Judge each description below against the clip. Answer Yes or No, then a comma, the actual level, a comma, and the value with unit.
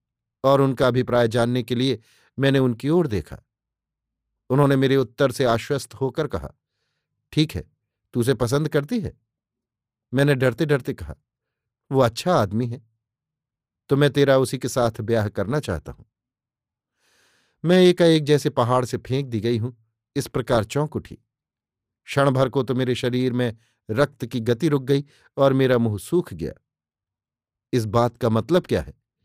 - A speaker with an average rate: Yes, average, 160 wpm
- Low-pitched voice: Yes, low, 125 Hz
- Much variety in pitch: No, average, 3.1 semitones